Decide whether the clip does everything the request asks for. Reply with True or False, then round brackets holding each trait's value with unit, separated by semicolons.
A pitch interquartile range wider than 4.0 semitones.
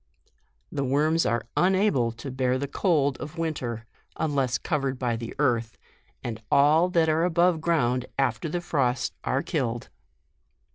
True (4.5 semitones)